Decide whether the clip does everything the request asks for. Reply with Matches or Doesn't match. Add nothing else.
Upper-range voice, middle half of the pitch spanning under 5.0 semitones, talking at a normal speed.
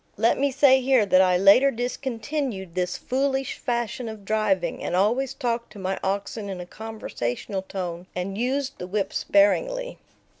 Doesn't match